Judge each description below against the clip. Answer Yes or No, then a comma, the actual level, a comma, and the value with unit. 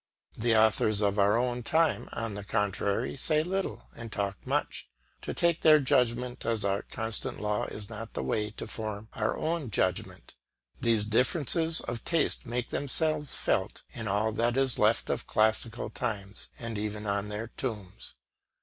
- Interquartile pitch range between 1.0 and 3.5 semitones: Yes, average, 3.2 semitones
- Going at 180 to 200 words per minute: No, average, 165 wpm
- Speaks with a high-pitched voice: No, low, 115 Hz